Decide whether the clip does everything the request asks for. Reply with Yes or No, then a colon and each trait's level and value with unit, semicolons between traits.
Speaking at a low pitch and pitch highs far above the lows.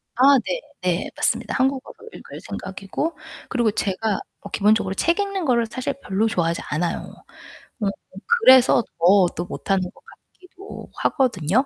No: high, 225 Hz; wide, 6.3 semitones